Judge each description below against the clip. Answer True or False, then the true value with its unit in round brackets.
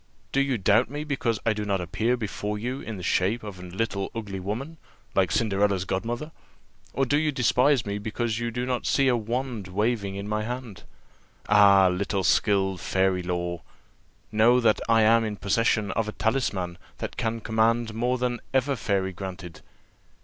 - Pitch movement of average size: True (3.7 semitones)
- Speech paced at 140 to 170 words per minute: False (180 wpm)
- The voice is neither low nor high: False (110 Hz)